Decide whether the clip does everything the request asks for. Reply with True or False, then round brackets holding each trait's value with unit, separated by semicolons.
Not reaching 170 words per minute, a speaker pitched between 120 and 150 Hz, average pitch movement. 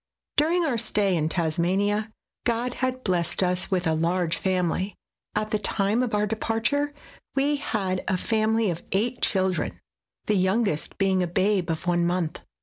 False (160 wpm; 195 Hz; 4.0 semitones)